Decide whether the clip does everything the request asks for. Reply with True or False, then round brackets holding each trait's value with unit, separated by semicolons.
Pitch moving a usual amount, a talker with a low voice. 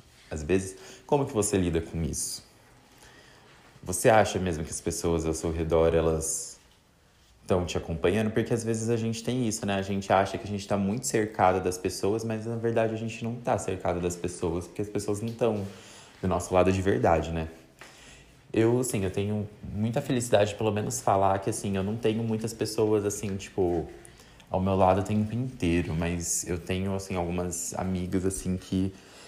True (3.7 semitones; 95 Hz)